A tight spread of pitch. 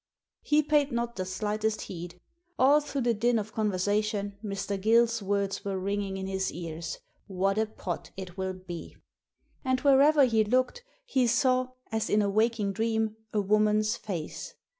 No: average, 3.4 semitones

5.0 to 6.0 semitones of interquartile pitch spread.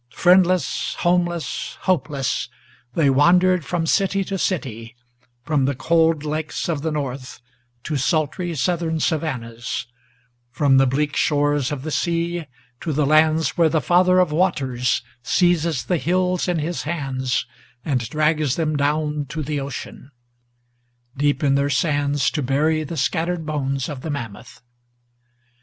No: average, 3.5 semitones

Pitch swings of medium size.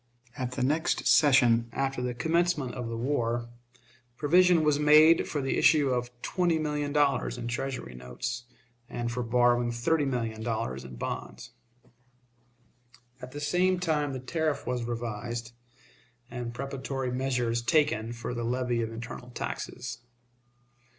Yes: average, 3.8 semitones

